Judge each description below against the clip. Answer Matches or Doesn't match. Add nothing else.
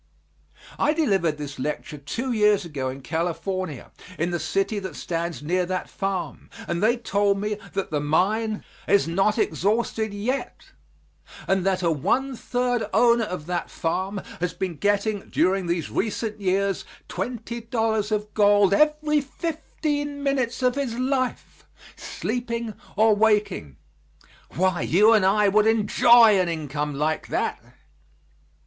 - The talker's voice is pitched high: Matches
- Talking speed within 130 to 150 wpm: Matches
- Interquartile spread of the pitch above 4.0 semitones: Matches